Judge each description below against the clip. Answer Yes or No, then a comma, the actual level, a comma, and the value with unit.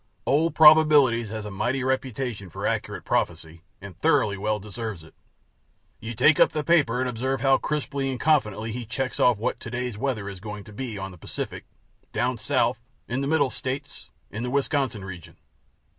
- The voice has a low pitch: Yes, low, 125 Hz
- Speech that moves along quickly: No, average, 185 wpm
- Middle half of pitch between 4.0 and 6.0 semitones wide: Yes, average, 4.6 semitones